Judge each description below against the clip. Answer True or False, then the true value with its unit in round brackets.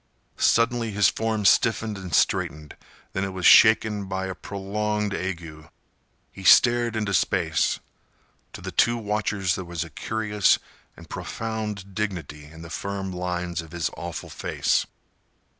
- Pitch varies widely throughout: False (3.4 semitones)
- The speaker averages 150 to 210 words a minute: False (140 wpm)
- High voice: False (95 Hz)